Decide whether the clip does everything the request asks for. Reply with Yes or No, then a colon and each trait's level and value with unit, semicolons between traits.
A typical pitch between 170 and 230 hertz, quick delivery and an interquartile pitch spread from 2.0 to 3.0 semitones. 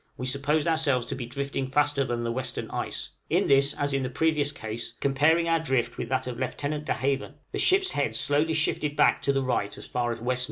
No: medium, 140 Hz; fast, 230 wpm; average, 2.7 semitones